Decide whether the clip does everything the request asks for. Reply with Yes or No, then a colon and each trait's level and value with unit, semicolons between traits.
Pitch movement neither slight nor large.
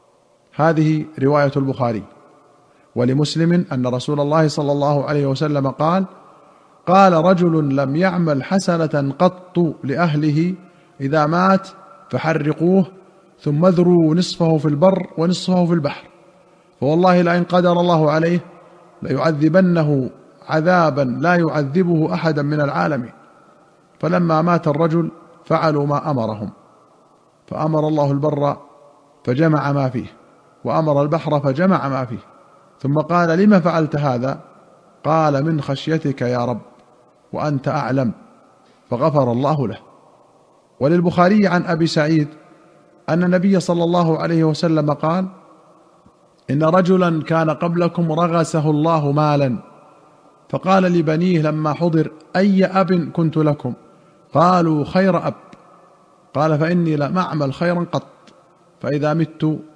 Yes: average, 3.3 semitones